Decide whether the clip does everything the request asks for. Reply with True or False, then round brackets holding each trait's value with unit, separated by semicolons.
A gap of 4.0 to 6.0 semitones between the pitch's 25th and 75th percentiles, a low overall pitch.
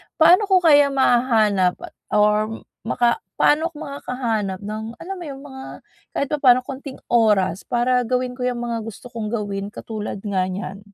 False (4.3 semitones; 240 Hz)